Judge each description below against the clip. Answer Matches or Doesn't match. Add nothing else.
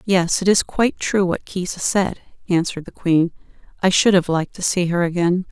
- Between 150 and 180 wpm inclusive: Doesn't match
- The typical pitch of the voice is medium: Matches